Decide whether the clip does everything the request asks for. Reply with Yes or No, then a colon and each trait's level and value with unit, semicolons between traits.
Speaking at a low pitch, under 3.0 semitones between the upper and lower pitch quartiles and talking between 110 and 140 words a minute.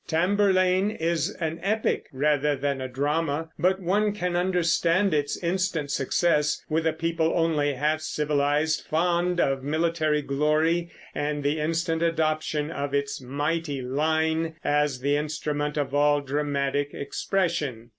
No: medium, 155 Hz; narrow, 2.6 semitones; slow, 135 wpm